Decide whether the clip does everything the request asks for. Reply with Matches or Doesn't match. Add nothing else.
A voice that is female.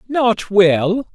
Doesn't match